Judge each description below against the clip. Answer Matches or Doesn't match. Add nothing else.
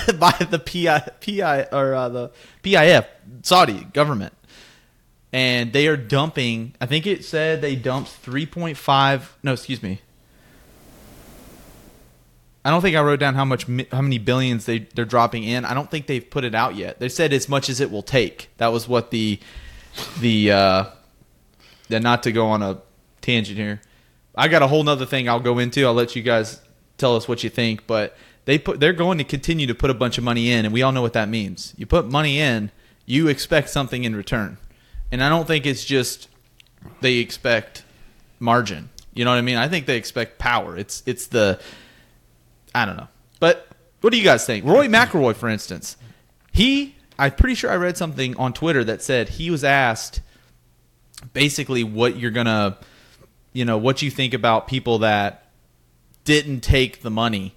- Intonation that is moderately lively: Matches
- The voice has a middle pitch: Doesn't match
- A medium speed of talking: Matches